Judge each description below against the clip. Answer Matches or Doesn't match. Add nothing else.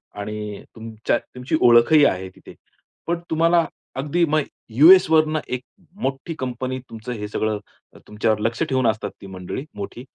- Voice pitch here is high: Doesn't match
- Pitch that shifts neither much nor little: Doesn't match